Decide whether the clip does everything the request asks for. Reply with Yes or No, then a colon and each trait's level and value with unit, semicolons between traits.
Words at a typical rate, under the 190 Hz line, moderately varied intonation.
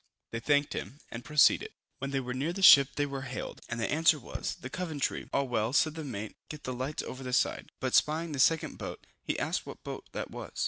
No: fast, 235 wpm; medium, 140 Hz; average, 3.1 semitones